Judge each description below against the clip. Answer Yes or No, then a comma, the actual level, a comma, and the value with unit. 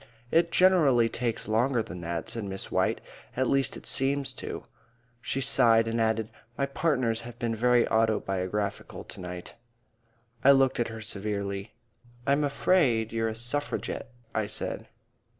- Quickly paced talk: No, average, 150 wpm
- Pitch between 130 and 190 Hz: No, low, 115 Hz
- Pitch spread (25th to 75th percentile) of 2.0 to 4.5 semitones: Yes, average, 3.8 semitones